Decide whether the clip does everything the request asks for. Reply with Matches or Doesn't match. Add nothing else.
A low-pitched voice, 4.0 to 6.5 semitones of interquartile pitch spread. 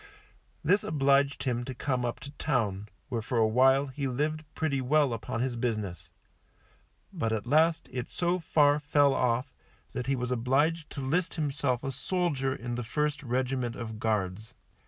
Doesn't match